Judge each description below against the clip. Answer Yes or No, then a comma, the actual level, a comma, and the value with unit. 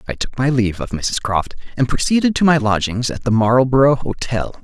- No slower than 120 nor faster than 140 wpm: No, fast, 205 wpm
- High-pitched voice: No, low, 125 Hz